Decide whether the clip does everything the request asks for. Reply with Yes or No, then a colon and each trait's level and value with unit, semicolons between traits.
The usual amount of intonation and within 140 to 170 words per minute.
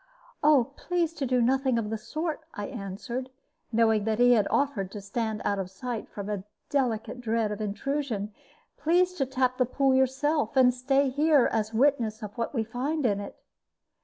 No: average, 4.1 semitones; average, 180 wpm